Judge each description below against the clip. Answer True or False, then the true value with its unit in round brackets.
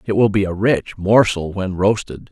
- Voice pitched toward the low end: True (100 Hz)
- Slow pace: False (205 wpm)